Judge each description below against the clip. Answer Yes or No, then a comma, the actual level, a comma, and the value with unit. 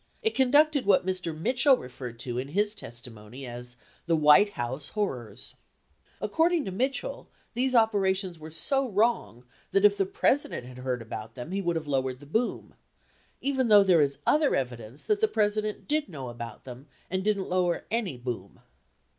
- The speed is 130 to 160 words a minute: No, average, 175 wpm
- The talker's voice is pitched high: No, medium, 180 Hz